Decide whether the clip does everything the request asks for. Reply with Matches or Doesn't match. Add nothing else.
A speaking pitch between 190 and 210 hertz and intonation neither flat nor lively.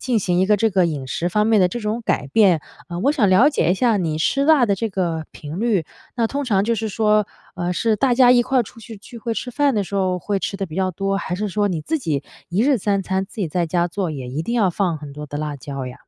Matches